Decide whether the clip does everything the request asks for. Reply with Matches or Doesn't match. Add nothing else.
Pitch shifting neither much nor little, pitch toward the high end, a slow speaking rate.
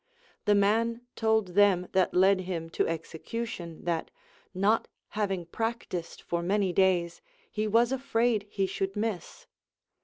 Matches